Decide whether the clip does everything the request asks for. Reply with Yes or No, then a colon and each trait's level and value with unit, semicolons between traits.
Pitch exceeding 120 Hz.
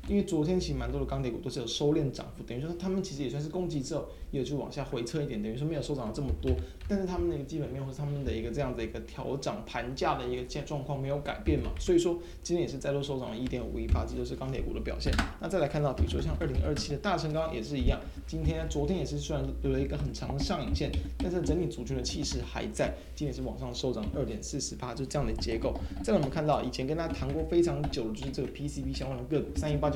Yes: medium, 140 Hz